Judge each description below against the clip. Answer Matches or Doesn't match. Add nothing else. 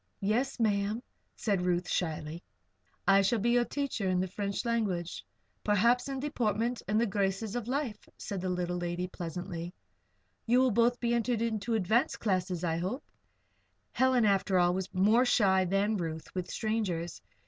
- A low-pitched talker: Doesn't match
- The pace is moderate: Matches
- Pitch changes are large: Doesn't match